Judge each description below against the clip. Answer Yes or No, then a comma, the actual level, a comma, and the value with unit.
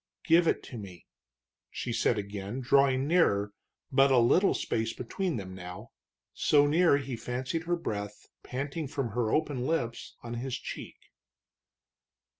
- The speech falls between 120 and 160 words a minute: Yes, average, 145 wpm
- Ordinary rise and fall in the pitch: Yes, average, 4.6 semitones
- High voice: No, low, 130 Hz